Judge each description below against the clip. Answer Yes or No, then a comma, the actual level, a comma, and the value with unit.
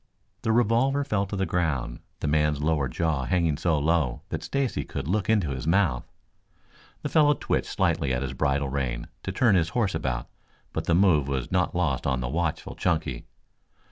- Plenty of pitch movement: Yes, wide, 6.0 semitones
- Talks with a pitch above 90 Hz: No, very low, 80 Hz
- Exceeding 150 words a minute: Yes, average, 185 wpm